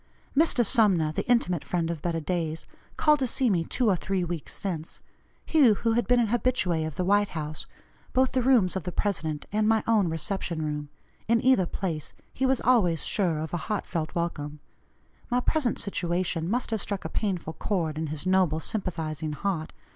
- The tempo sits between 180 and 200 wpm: Yes, average, 190 wpm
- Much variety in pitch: Yes, wide, 5.7 semitones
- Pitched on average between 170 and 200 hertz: Yes, medium, 185 Hz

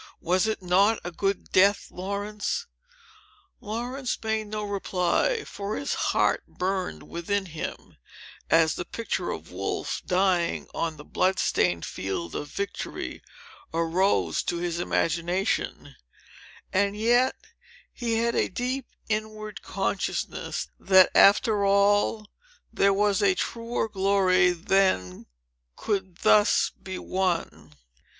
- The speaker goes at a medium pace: No, slow, 115 wpm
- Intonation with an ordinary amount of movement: Yes, average, 3.2 semitones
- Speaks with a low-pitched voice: No, high, 195 Hz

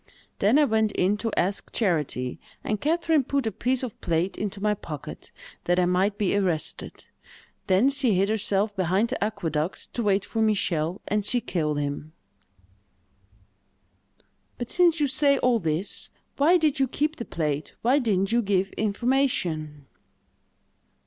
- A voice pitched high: Yes, high, 205 Hz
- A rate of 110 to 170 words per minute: Yes, average, 150 wpm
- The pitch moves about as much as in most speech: No, wide, 5.7 semitones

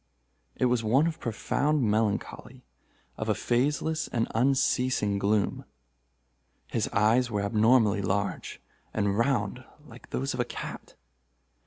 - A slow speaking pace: Yes, slow, 120 wpm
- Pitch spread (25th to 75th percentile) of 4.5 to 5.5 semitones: No, average, 3.7 semitones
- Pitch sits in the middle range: No, low, 115 Hz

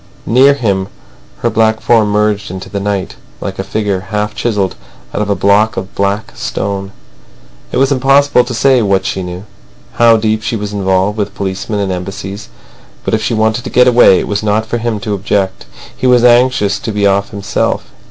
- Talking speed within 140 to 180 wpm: No, average, 195 wpm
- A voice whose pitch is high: No, low, 105 Hz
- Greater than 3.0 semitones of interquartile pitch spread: No, narrow, 2.5 semitones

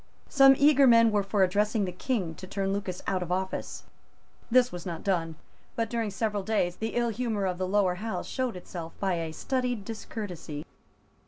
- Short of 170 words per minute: No, average, 185 wpm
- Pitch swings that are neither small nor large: Yes, average, 4.1 semitones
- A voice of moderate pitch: No, high, 200 Hz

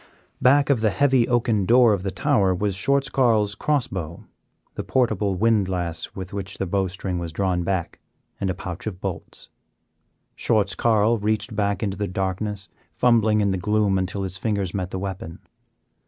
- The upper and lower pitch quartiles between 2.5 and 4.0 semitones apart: Yes, average, 2.9 semitones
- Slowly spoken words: No, average, 170 wpm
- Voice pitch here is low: Yes, low, 100 Hz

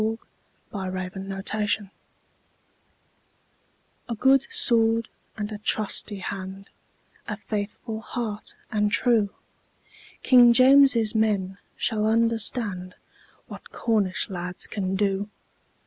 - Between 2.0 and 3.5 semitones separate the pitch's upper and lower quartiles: Yes, average, 2.9 semitones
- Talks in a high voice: Yes, high, 210 Hz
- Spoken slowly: Yes, slow, 85 wpm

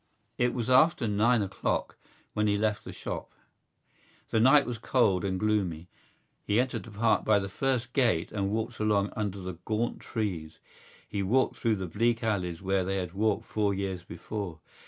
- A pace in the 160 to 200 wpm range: Yes, average, 175 wpm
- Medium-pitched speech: No, low, 105 Hz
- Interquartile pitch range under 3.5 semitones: Yes, average, 3.0 semitones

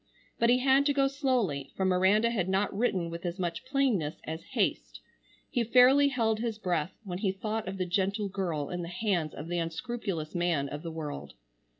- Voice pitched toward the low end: No, high, 190 Hz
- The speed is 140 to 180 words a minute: No, average, 200 wpm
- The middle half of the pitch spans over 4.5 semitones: Yes, wide, 5.6 semitones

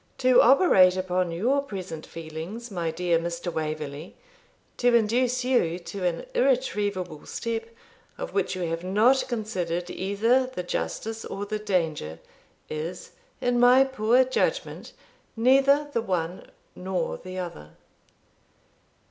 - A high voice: Yes, high, 195 Hz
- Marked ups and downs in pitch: Yes, wide, 6.1 semitones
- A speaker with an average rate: No, slow, 125 wpm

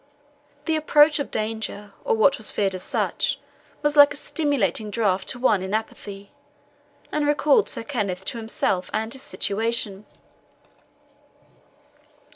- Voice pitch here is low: No, high, 220 Hz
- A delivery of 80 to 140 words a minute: Yes, slow, 135 wpm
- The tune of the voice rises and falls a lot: Yes, wide, 6.1 semitones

